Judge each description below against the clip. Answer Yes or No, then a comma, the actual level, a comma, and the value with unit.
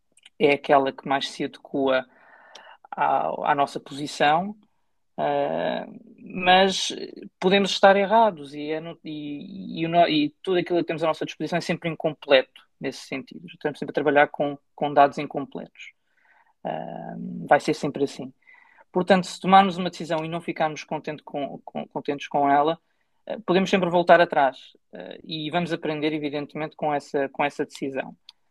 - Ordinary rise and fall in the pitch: Yes, average, 3.8 semitones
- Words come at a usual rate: Yes, average, 160 wpm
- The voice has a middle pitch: Yes, medium, 160 Hz